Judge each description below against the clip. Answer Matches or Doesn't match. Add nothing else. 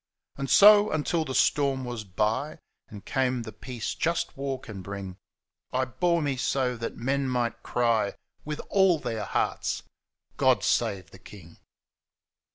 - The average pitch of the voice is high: Doesn't match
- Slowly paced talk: Doesn't match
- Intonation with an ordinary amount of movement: Matches